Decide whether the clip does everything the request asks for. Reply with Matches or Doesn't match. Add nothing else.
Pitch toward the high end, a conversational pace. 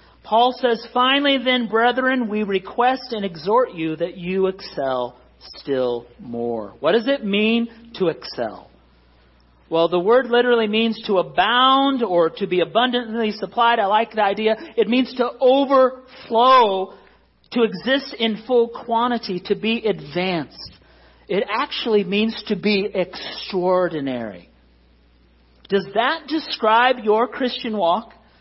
Doesn't match